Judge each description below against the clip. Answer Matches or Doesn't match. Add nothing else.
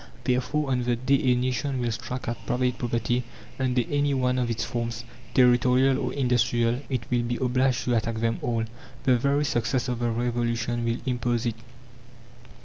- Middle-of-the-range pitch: Doesn't match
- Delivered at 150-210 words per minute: Matches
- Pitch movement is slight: Matches